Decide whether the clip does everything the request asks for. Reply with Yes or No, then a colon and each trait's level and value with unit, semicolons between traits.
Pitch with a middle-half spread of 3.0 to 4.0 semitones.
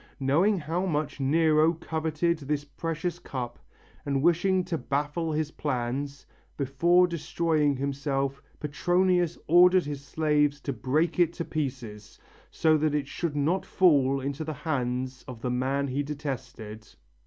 Yes: average, 3.3 semitones